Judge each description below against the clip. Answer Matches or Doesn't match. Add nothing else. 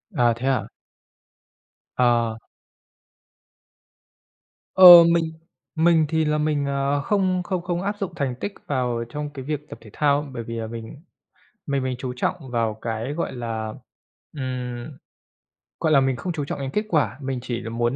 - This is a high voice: Doesn't match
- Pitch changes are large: Doesn't match